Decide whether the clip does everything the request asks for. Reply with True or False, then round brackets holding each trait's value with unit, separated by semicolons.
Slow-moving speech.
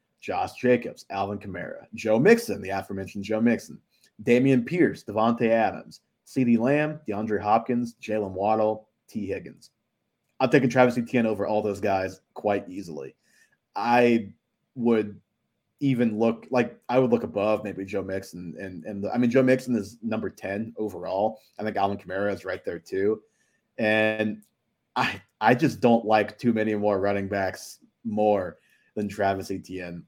False (150 wpm)